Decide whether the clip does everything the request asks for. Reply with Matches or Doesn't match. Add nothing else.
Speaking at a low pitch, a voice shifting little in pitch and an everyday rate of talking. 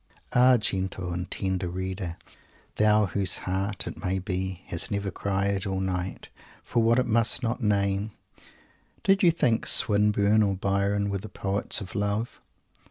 Matches